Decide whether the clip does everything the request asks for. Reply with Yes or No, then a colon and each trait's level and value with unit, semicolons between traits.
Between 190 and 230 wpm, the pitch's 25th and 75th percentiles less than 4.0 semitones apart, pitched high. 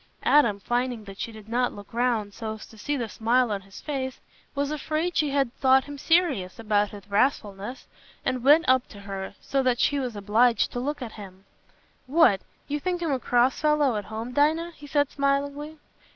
No: average, 200 wpm; average, 5.1 semitones; very high, 250 Hz